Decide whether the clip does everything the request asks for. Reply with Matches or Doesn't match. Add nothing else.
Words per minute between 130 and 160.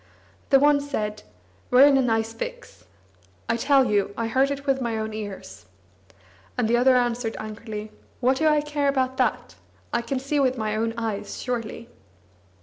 Doesn't match